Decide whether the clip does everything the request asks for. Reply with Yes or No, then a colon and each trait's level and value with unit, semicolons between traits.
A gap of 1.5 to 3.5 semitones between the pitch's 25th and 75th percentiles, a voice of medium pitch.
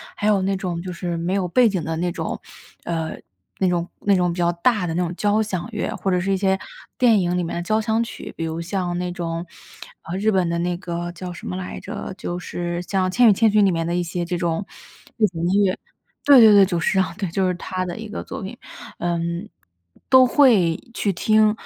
Yes: average, 2.9 semitones; medium, 180 Hz